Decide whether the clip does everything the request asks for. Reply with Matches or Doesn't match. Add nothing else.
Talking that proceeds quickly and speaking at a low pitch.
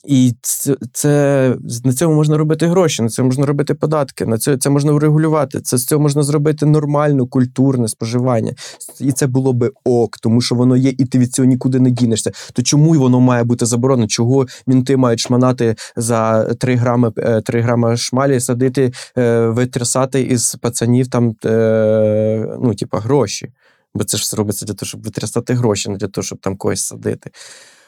Matches